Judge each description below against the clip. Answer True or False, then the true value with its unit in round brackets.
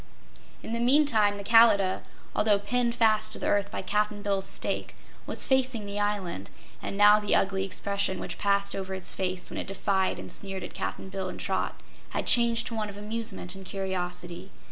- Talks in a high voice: True (200 Hz)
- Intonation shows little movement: True (2.1 semitones)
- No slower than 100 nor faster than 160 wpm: False (190 wpm)